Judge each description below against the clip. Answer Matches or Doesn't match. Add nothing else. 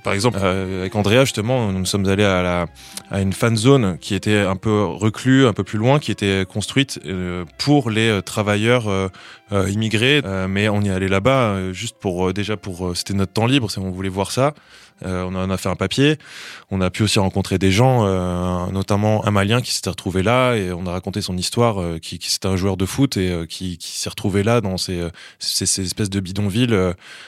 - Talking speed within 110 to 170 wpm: Doesn't match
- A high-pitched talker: Doesn't match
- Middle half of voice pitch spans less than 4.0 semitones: Matches